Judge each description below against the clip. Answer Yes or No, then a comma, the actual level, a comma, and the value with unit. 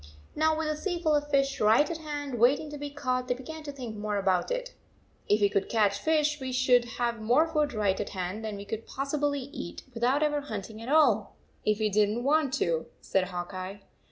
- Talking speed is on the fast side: Yes, fast, 235 wpm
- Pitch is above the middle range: Yes, very high, 250 Hz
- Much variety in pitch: Yes, wide, 5.8 semitones